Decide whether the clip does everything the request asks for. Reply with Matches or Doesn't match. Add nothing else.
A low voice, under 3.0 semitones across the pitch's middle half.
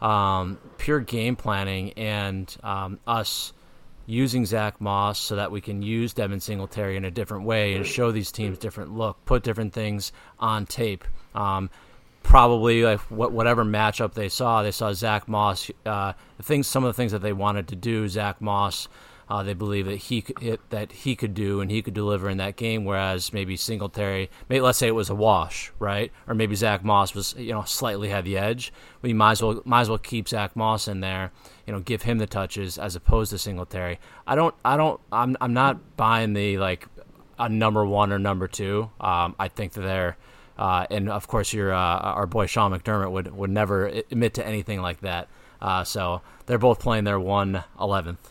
Matches